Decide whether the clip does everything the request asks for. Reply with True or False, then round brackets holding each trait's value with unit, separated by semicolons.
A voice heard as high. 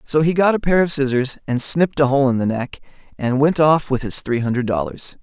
False (140 Hz)